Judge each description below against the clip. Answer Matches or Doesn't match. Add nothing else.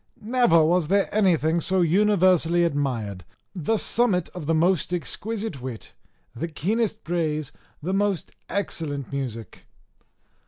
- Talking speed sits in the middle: Doesn't match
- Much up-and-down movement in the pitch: Doesn't match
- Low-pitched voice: Doesn't match